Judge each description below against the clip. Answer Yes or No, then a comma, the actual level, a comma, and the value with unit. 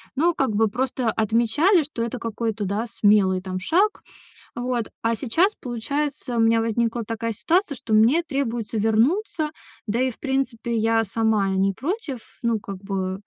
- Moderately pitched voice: No, high, 230 Hz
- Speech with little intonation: No, average, 3.8 semitones